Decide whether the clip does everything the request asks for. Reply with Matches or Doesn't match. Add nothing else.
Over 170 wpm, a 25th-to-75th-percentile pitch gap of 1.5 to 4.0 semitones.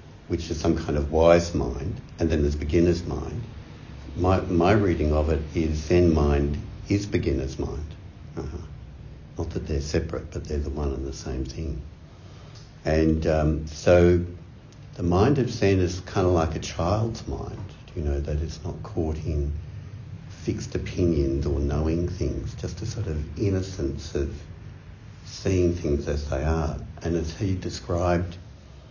Doesn't match